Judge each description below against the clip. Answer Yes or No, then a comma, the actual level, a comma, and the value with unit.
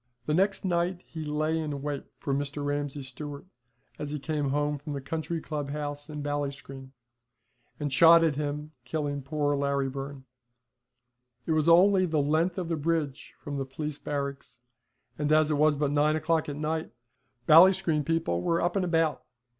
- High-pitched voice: No, medium, 150 Hz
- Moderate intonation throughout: No, narrow, 2.1 semitones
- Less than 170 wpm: No, average, 175 wpm